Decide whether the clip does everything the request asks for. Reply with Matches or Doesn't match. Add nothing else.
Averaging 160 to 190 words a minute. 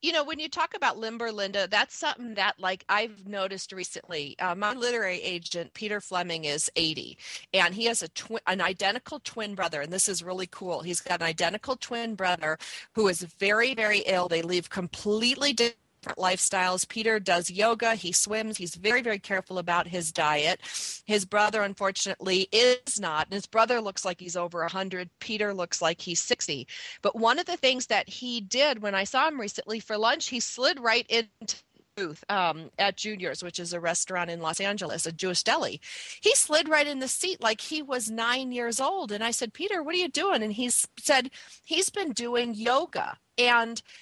Doesn't match